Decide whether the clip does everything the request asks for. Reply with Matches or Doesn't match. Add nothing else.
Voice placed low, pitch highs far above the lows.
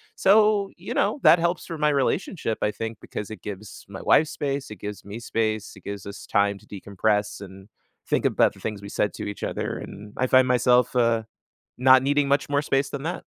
Matches